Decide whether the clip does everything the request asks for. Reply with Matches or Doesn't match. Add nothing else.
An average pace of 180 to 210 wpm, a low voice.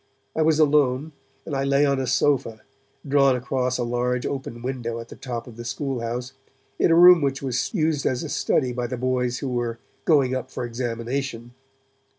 Matches